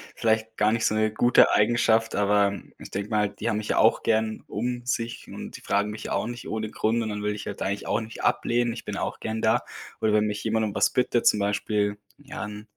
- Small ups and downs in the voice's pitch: Yes, narrow, 1.6 semitones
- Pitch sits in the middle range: No, low, 110 Hz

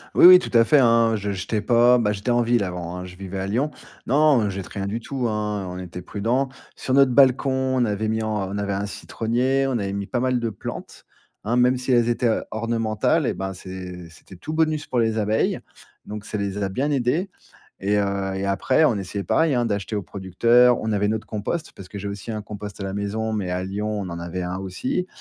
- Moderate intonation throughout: Yes, average, 3.8 semitones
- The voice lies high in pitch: No, low, 105 Hz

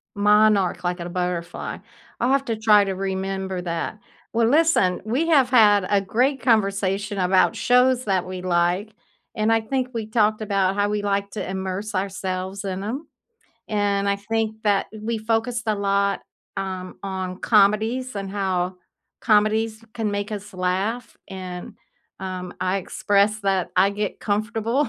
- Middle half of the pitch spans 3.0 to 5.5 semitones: No, narrow, 2.6 semitones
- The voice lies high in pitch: Yes, high, 205 Hz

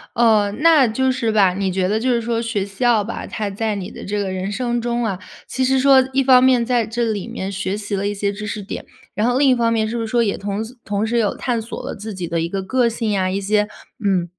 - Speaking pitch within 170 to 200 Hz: No, high, 220 Hz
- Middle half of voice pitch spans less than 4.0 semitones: Yes, average, 3.1 semitones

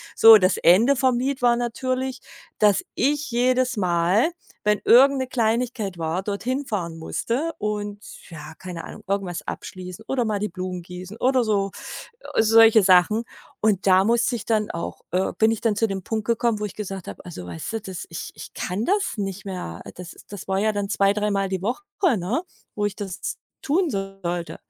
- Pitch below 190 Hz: No, high, 210 Hz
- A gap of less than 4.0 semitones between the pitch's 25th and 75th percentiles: No, average, 4.3 semitones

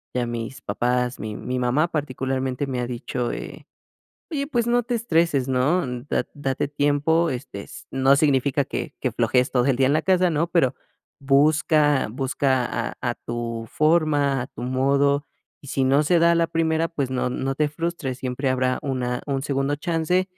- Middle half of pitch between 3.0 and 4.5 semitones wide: Yes, average, 3.6 semitones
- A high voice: No, low, 135 Hz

